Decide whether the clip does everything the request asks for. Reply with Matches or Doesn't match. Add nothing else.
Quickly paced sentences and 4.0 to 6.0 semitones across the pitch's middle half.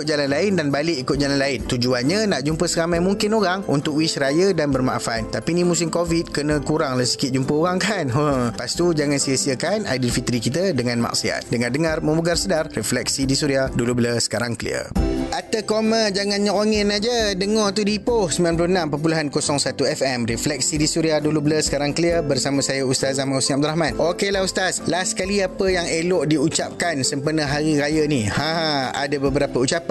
Matches